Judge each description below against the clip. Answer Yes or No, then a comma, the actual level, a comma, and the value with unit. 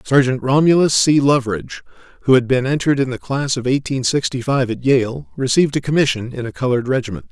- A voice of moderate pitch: No, low, 130 Hz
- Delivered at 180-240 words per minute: Yes, average, 195 wpm